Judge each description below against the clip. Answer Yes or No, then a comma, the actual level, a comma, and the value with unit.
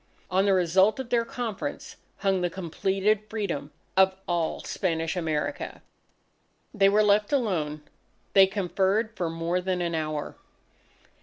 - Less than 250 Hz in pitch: Yes, high, 190 Hz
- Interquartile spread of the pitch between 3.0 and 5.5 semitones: Yes, average, 3.7 semitones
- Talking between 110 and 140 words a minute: Yes, slow, 135 wpm